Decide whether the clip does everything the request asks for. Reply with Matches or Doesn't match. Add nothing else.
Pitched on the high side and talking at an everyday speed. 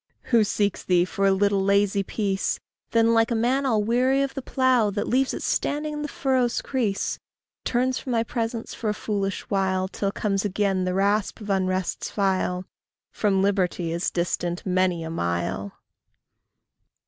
Matches